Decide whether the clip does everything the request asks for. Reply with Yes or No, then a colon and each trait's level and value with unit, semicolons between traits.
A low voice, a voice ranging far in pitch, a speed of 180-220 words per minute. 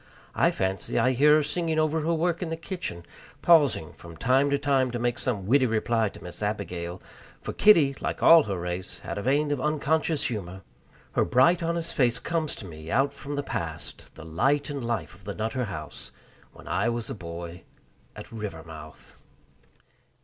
Yes: low, 125 Hz; wide, 7.8 semitones; average, 185 wpm